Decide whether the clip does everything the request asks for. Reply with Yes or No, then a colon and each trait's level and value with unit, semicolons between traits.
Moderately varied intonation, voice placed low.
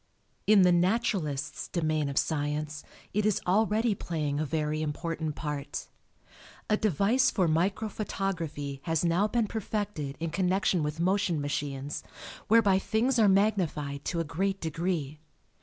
No: average, 5.0 semitones; medium, 170 Hz